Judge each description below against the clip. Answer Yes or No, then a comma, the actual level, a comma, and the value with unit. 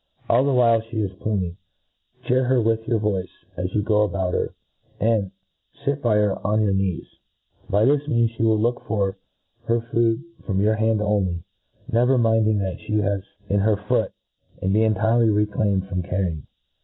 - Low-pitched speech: Yes, low, 105 Hz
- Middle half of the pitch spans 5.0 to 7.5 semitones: No, narrow, 2.6 semitones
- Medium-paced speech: Yes, average, 185 wpm